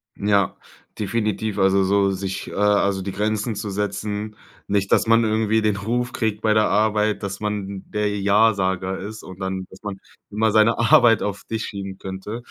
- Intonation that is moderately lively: No, narrow, 1.9 semitones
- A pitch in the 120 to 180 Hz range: No, low, 105 Hz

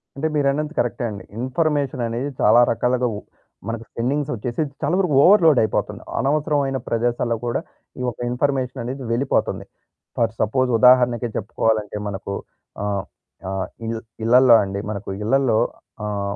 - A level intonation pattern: No, average, 3.5 semitones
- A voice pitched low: Yes, low, 125 Hz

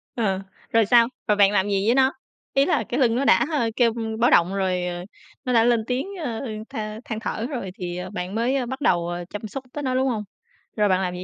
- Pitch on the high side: Yes, high, 220 Hz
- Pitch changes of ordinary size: Yes, average, 4.6 semitones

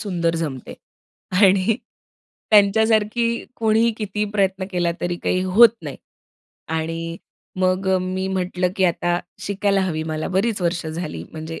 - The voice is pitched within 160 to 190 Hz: Yes, medium, 185 Hz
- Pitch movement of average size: Yes, average, 3.3 semitones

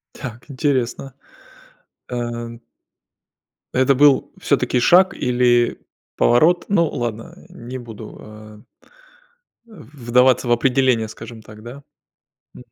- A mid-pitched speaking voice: No, low, 120 Hz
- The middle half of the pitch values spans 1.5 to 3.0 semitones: Yes, narrow, 2.4 semitones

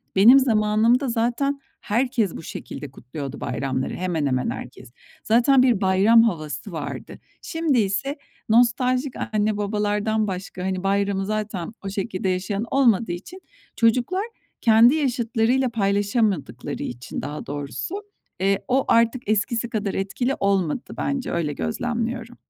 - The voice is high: Yes, high, 215 Hz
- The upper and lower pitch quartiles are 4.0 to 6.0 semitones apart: Yes, average, 4.3 semitones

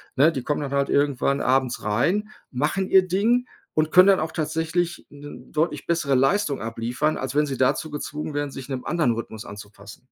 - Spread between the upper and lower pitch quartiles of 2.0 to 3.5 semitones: No, average, 4.0 semitones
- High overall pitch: No, medium, 145 Hz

